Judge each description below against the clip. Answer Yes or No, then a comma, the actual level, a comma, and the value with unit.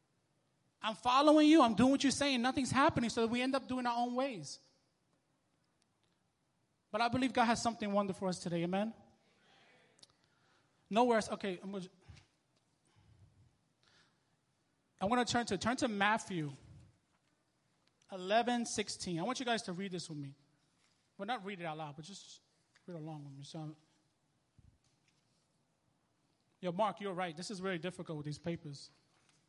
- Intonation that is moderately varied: No, wide, 7.1 semitones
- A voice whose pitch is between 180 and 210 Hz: Yes, medium, 185 Hz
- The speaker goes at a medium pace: Yes, average, 160 wpm